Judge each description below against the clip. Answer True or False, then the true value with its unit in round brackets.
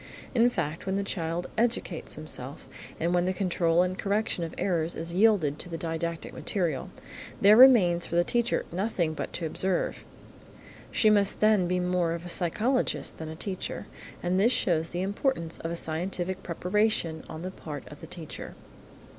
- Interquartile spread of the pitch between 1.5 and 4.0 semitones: True (3.2 semitones)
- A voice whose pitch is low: False (180 Hz)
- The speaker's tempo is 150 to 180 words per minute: True (175 wpm)